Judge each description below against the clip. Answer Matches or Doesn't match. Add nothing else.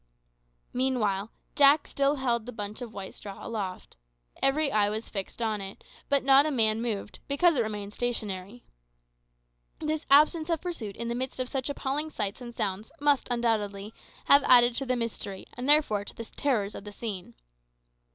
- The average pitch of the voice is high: Matches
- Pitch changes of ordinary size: Matches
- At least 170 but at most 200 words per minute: Matches